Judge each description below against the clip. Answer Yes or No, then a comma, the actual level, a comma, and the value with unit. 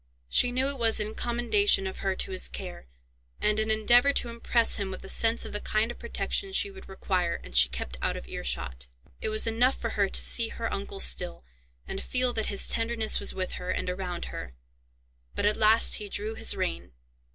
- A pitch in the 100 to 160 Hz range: No, high, 215 Hz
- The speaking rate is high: Yes, fast, 215 wpm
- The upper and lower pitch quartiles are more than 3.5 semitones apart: Yes, average, 4.0 semitones